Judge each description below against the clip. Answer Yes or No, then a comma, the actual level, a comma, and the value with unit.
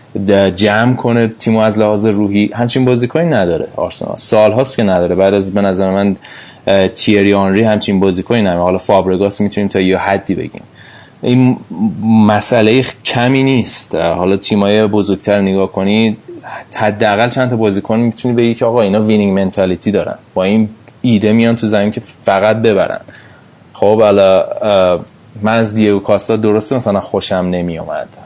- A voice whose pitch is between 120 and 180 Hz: No, low, 105 Hz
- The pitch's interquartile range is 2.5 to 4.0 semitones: Yes, average, 2.9 semitones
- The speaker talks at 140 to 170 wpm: Yes, average, 150 wpm